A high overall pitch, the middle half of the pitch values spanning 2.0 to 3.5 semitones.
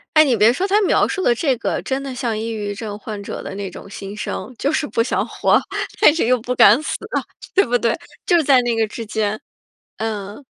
No: high, 230 Hz; average, 4.3 semitones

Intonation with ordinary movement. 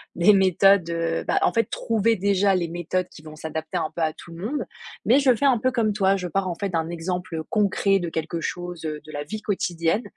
Yes: average, 3.5 semitones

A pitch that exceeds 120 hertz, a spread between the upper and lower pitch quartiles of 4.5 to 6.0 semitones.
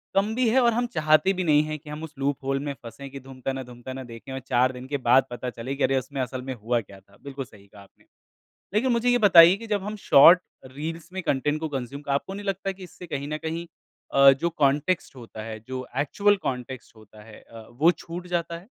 Yes: medium, 140 Hz; average, 5.2 semitones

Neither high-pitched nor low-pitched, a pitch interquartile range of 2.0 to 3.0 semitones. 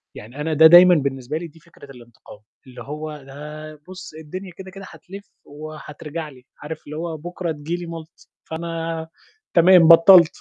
Yes: medium, 160 Hz; narrow, 2.4 semitones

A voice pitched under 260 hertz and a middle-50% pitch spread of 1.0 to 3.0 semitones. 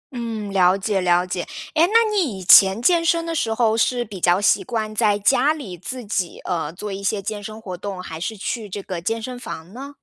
No: high, 210 Hz; average, 4.6 semitones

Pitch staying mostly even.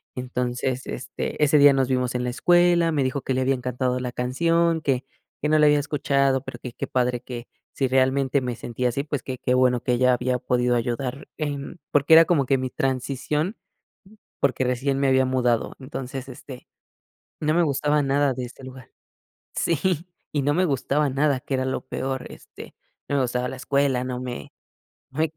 Yes: narrow, 2.3 semitones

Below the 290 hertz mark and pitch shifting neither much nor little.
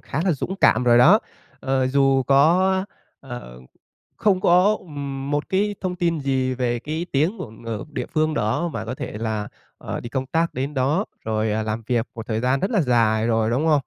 No: low, 135 Hz; wide, 6.1 semitones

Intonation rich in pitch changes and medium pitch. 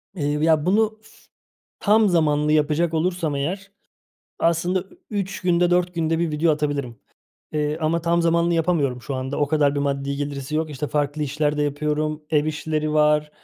No: narrow, 2.5 semitones; medium, 155 Hz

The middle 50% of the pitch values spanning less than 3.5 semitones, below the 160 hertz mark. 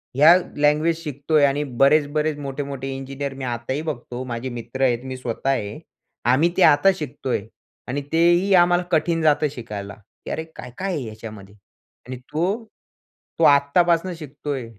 No: average, 3.8 semitones; medium, 140 Hz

